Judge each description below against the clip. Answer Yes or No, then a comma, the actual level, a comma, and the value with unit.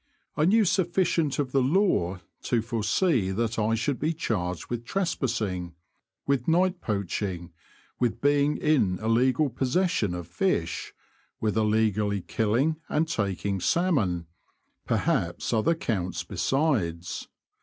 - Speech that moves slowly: Yes, slow, 125 wpm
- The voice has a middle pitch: No, low, 115 Hz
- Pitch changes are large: Yes, wide, 7.6 semitones